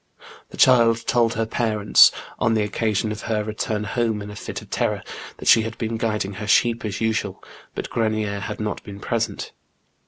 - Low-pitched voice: Yes, low, 110 Hz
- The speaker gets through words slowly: No, average, 190 wpm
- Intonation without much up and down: Yes, narrow, 1.5 semitones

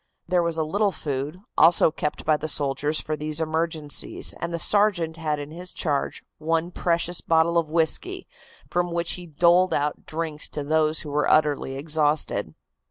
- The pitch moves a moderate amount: No, narrow, 2.2 semitones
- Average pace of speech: Yes, average, 170 wpm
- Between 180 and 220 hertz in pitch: No, medium, 160 Hz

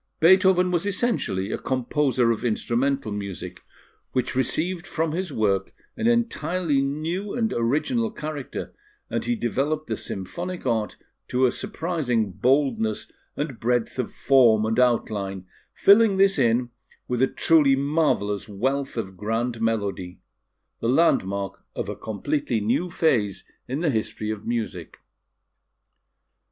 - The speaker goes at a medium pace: No, slow, 130 wpm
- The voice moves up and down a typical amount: No, wide, 6.9 semitones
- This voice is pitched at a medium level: No, low, 130 Hz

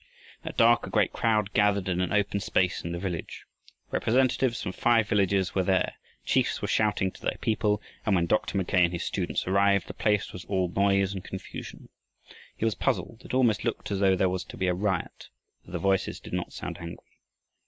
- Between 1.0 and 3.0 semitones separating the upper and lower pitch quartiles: Yes, narrow, 2.4 semitones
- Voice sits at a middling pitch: No, low, 100 Hz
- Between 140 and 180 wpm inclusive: No, fast, 205 wpm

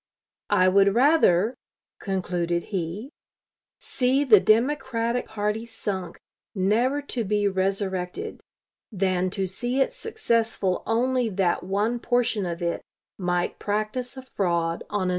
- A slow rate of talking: Yes, slow, 120 wpm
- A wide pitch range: No, average, 4.6 semitones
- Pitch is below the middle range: No, high, 210 Hz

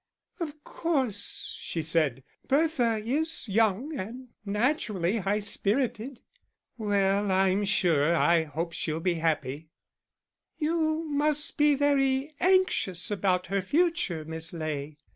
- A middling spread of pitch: No, wide, 9.0 semitones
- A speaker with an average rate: No, slow, 115 wpm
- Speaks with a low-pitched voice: No, high, 205 Hz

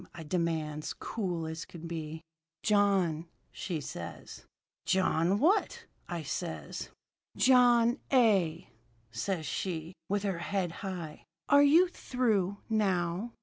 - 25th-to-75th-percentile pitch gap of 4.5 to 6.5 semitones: Yes, average, 4.9 semitones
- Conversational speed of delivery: No, slow, 110 wpm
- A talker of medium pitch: Yes, medium, 180 Hz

